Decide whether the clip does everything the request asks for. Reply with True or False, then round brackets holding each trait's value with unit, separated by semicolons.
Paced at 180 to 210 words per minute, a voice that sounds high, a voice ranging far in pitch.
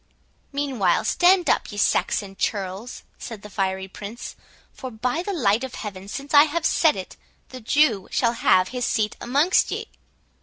False (165 wpm; 235 Hz; 6.2 semitones)